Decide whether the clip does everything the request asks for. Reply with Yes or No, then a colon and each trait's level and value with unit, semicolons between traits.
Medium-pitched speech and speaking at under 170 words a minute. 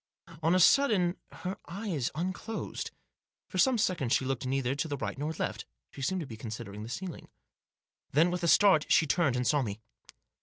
No: medium, 155 Hz; average, 190 wpm